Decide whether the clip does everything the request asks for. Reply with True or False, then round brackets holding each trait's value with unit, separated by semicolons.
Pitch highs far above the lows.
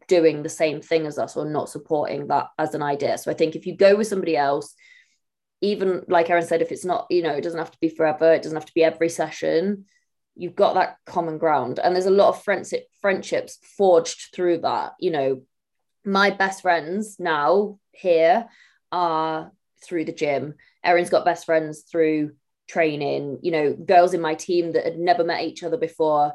False (3.4 semitones)